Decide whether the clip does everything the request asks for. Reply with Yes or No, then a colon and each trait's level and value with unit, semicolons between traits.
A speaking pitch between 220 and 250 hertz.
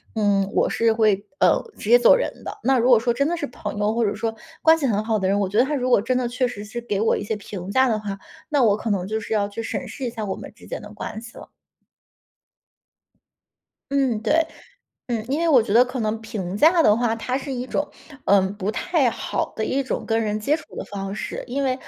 Yes: high, 225 Hz